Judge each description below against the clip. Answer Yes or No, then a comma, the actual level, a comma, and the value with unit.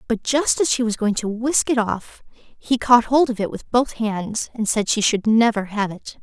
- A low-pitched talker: No, high, 225 Hz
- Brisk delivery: Yes, fast, 240 wpm